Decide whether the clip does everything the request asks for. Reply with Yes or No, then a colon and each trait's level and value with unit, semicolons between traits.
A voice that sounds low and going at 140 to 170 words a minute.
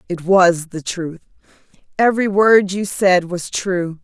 No: medium, 185 Hz; average, 150 wpm